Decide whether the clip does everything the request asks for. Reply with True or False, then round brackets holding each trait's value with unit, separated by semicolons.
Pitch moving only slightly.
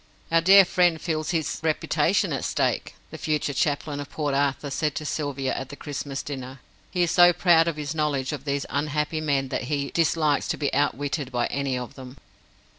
True (2.3 semitones)